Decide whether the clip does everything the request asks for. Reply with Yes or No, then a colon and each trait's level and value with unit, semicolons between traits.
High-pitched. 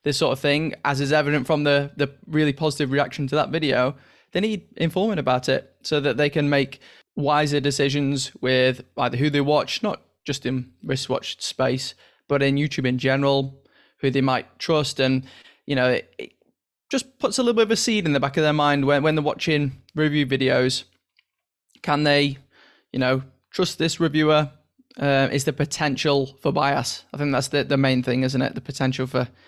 No: medium, 140 Hz